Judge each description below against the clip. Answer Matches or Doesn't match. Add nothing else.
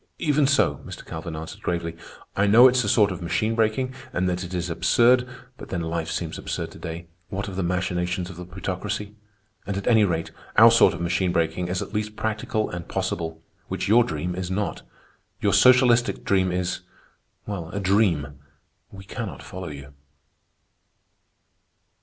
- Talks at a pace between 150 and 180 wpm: Matches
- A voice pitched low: Matches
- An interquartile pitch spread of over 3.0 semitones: Matches